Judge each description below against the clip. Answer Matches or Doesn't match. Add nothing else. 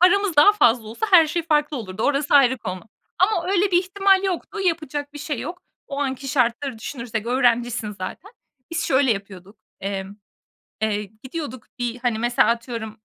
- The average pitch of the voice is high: Matches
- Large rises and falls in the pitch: Matches